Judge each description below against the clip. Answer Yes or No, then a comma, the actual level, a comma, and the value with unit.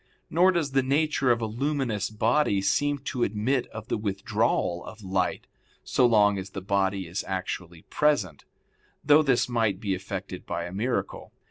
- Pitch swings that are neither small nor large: No, wide, 5.8 semitones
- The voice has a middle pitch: No, low, 110 Hz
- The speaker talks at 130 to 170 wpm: Yes, average, 165 wpm